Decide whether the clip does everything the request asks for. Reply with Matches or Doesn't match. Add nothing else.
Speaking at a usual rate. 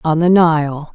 Matches